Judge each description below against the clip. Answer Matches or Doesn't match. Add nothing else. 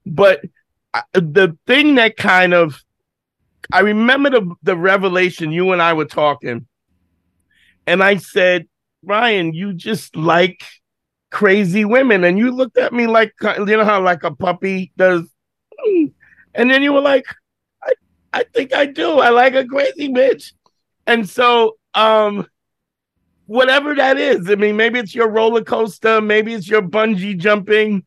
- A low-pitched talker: Doesn't match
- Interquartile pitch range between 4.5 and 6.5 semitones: Matches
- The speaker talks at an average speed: Matches